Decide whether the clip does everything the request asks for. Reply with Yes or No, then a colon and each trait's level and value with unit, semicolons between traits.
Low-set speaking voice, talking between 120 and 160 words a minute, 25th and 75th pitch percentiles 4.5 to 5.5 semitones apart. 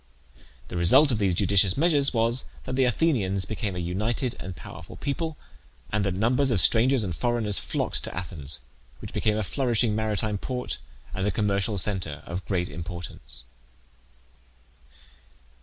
Yes: low, 105 Hz; average, 150 wpm; average, 4.8 semitones